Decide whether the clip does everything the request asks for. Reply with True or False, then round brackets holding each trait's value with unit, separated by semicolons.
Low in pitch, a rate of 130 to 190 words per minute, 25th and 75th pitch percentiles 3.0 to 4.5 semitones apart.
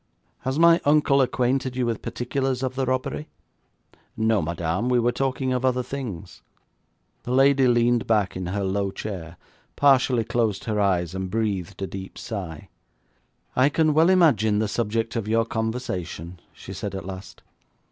False (115 Hz; 160 wpm; 5.0 semitones)